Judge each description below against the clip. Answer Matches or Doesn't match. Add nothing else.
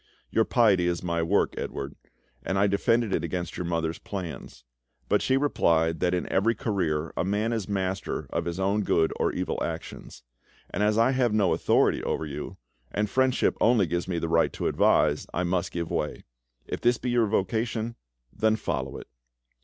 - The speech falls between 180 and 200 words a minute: Matches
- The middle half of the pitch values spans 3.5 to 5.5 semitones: Matches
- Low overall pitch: Matches